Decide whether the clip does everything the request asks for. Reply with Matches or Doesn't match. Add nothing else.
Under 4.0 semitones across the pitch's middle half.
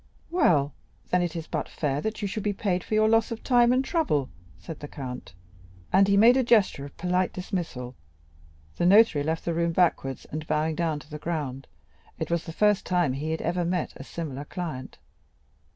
Doesn't match